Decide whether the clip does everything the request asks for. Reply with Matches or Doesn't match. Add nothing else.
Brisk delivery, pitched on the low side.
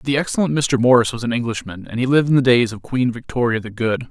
Matches